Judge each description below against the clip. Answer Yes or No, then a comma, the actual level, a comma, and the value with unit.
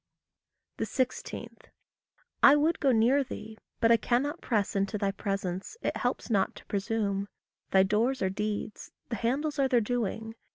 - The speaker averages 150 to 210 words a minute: Yes, average, 155 wpm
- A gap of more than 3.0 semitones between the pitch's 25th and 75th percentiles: Yes, average, 4.4 semitones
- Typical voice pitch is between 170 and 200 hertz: No, high, 225 Hz